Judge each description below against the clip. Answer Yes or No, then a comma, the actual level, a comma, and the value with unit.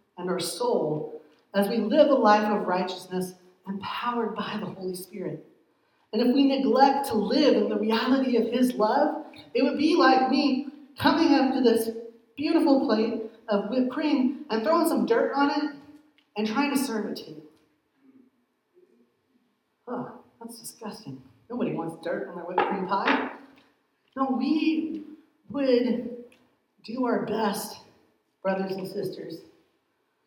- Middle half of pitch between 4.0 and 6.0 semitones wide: Yes, average, 5.0 semitones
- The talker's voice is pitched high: Yes, high, 240 Hz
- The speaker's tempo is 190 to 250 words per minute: No, average, 145 wpm